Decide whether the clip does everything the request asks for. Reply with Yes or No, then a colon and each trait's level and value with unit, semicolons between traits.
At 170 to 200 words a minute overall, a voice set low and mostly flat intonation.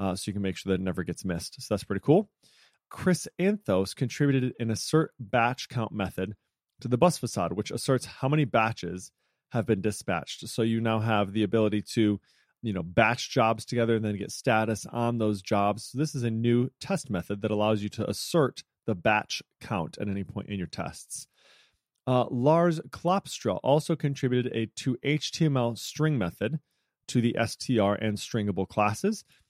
No: average, 185 wpm; low, 115 Hz; average, 4.4 semitones